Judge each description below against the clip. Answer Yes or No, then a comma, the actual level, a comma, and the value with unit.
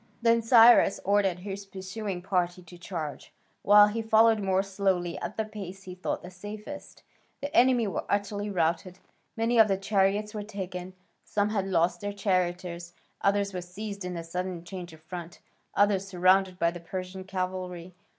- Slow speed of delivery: No, average, 170 wpm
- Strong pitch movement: No, narrow, 2.4 semitones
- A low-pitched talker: No, high, 190 Hz